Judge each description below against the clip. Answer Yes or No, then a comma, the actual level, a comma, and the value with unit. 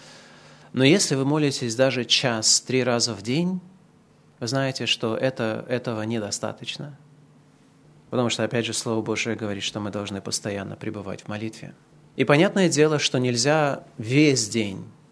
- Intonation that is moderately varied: Yes, average, 4.4 semitones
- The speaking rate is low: No, average, 145 wpm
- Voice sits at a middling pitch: No, low, 125 Hz